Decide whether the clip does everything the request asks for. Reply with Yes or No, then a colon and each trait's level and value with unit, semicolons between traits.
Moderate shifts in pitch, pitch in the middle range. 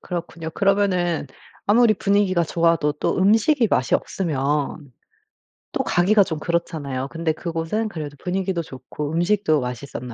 Yes: average, 4.6 semitones; medium, 170 Hz